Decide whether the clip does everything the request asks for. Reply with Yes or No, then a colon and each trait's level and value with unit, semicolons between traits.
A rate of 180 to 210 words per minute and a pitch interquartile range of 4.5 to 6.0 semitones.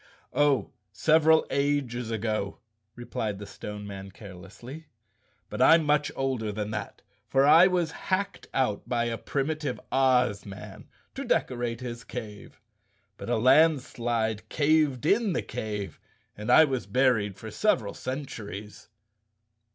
No: slow, 135 wpm; wide, 5.5 semitones